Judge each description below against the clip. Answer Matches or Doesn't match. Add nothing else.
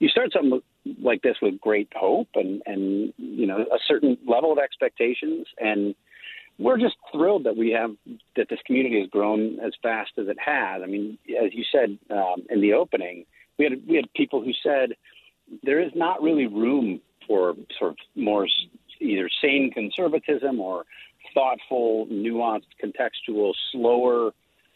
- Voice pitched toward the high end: Doesn't match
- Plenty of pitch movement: Matches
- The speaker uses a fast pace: Doesn't match